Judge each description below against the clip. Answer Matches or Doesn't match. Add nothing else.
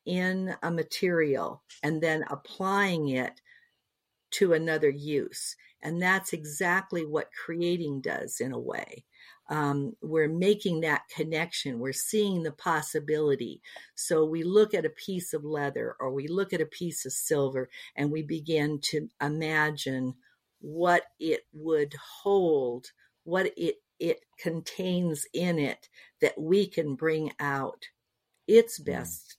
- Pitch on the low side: Doesn't match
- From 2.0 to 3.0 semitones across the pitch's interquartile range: Doesn't match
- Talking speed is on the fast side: Doesn't match